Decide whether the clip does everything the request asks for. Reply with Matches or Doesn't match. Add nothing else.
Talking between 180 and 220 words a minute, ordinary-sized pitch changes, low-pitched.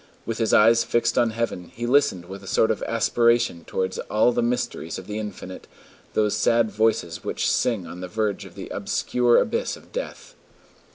Matches